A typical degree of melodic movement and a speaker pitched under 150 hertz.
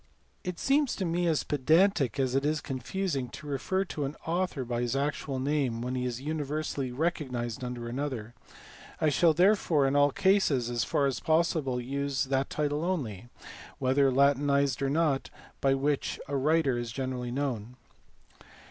Yes: average, 3.4 semitones; medium, 140 Hz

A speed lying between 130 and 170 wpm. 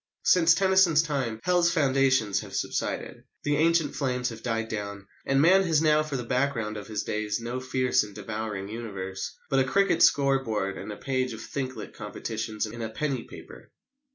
No: average, 180 wpm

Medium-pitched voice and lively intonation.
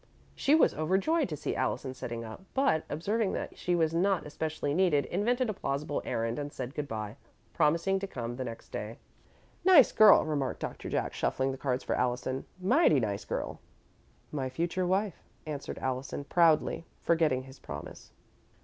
Yes: medium, 150 Hz; wide, 6.3 semitones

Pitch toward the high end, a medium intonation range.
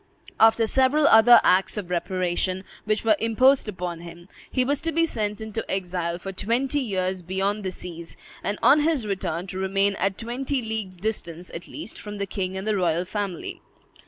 Yes: high, 200 Hz; average, 3.7 semitones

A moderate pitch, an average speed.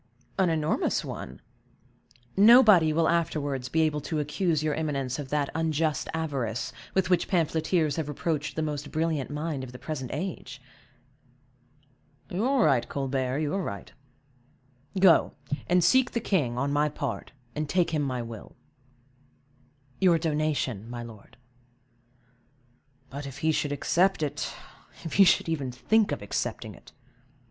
Yes: medium, 150 Hz; average, 145 wpm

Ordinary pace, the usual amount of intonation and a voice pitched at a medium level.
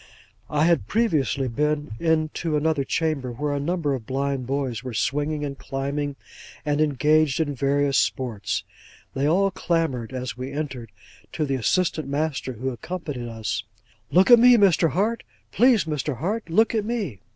Yes: average, 160 wpm; average, 3.7 semitones; medium, 145 Hz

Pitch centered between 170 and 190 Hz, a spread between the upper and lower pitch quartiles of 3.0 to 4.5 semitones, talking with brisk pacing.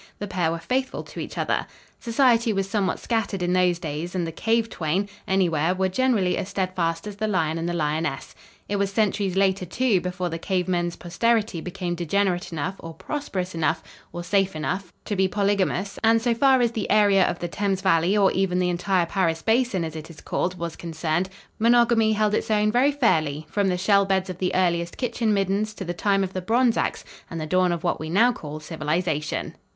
Yes: medium, 185 Hz; average, 3.5 semitones; fast, 210 wpm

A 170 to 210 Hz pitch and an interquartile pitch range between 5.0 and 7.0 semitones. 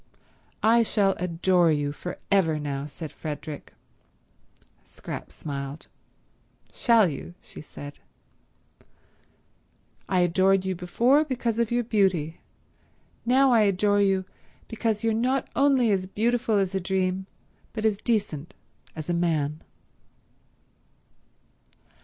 Yes: high, 190 Hz; wide, 5.4 semitones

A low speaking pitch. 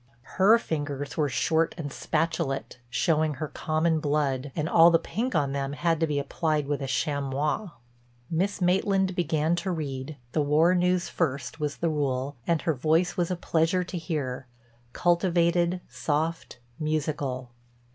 No: medium, 155 Hz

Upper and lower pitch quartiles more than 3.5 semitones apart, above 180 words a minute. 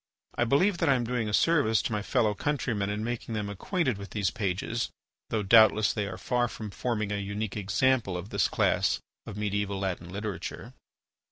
No: average, 3.1 semitones; average, 190 wpm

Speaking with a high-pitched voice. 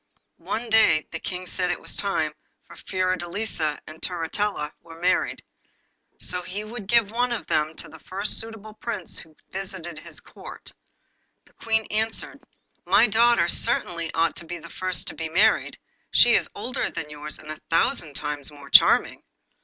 No: medium, 180 Hz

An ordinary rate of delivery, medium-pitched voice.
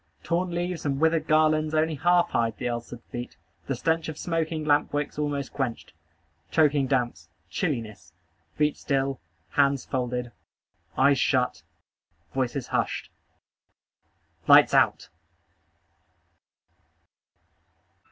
No: slow, 105 wpm; medium, 145 Hz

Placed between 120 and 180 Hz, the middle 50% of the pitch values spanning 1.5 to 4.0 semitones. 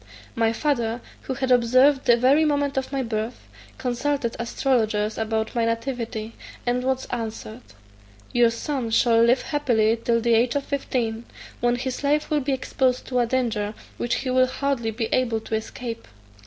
No: high, 240 Hz; narrow, 2.5 semitones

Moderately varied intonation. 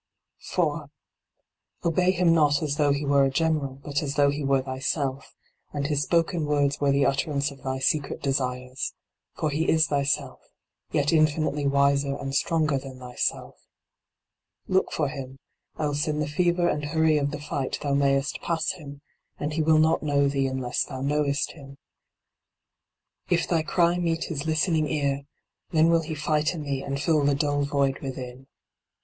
No: narrow, 2.1 semitones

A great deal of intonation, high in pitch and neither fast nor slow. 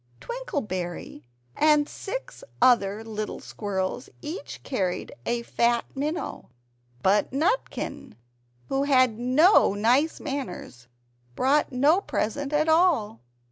No: wide, 6.3 semitones; very high, 255 Hz; slow, 100 wpm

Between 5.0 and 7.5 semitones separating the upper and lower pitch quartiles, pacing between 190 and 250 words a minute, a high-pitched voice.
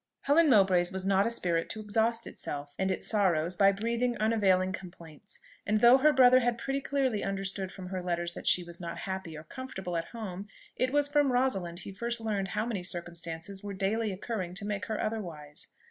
No: average, 4.5 semitones; average, 200 wpm; high, 195 Hz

